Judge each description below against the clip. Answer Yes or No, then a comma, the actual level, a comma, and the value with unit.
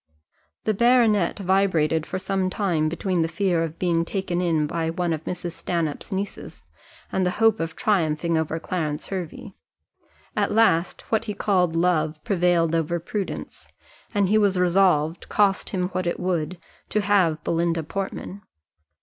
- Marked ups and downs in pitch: No, average, 3.0 semitones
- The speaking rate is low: No, average, 155 wpm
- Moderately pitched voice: Yes, medium, 180 Hz